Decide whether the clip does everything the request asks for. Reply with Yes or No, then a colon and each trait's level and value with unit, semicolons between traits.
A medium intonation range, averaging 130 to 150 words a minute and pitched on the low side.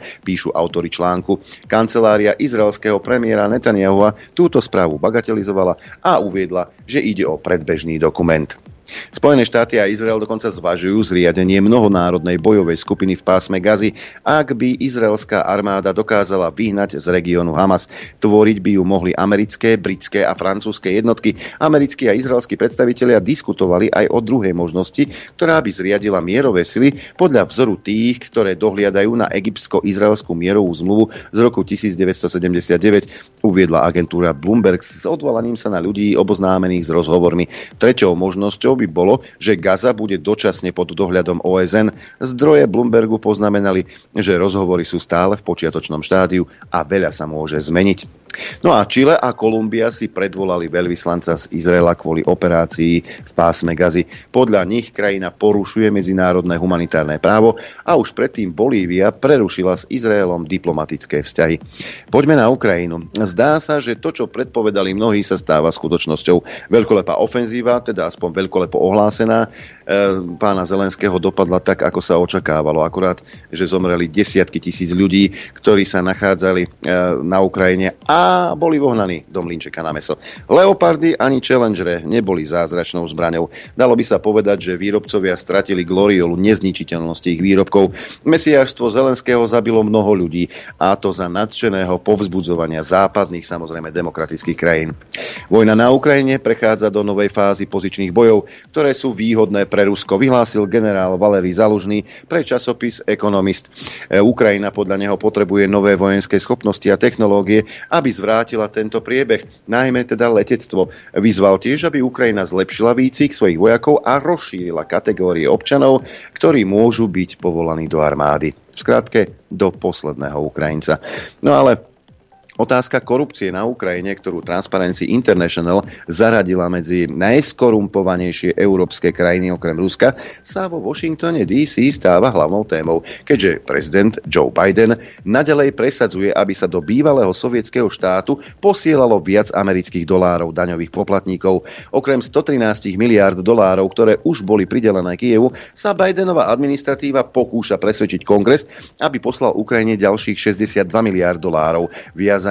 Yes: average, 4.0 semitones; average, 135 wpm; low, 100 Hz